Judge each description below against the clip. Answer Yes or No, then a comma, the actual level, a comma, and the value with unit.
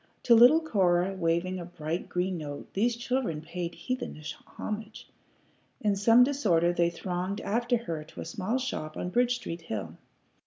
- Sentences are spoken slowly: No, average, 160 wpm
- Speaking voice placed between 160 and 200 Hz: Yes, medium, 185 Hz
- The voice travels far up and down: Yes, wide, 5.8 semitones